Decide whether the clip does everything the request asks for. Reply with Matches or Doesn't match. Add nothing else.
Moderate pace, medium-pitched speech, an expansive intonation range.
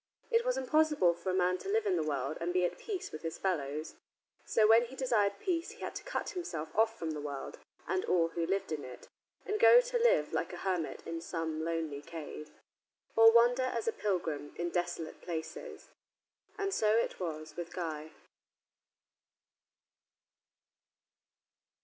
Matches